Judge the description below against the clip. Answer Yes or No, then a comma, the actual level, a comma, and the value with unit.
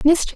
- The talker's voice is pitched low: No, very high, 320 Hz